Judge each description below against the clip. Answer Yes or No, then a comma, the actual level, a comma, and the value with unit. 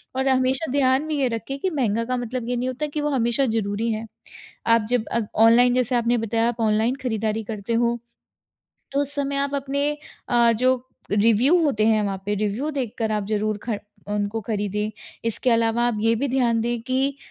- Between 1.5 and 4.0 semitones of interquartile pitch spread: Yes, average, 3.0 semitones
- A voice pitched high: Yes, high, 235 Hz